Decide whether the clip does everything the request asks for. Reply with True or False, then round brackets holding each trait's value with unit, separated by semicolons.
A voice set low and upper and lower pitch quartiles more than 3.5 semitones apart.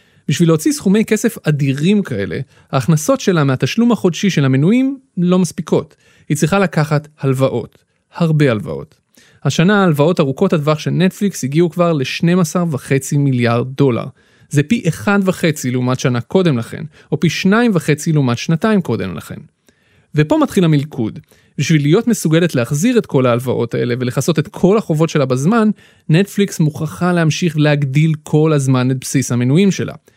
False (155 Hz; 5.2 semitones)